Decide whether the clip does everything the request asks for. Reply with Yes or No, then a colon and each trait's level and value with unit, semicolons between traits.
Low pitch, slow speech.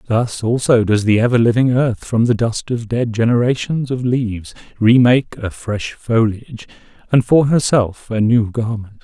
No: low, 115 Hz; average, 175 wpm